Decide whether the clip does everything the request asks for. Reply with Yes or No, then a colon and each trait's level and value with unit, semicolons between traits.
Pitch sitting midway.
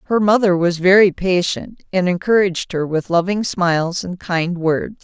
Yes: medium, 180 Hz